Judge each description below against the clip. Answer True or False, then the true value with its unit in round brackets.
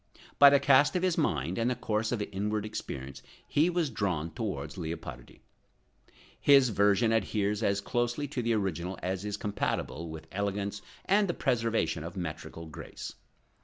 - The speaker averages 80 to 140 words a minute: False (165 wpm)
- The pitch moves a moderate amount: False (5.7 semitones)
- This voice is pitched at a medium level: False (105 Hz)